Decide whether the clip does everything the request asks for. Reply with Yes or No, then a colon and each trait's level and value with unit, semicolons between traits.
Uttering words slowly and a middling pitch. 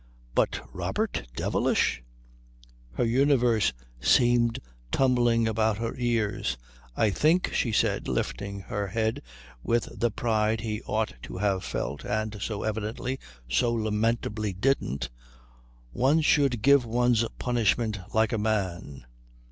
No: slow, 120 wpm; low, 110 Hz